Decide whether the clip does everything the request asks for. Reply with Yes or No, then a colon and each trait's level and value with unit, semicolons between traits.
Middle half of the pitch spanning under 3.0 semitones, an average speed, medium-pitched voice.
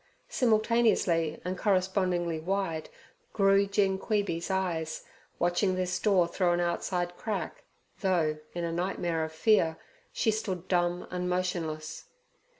No: narrow, 2.5 semitones; slow, 125 wpm; medium, 180 Hz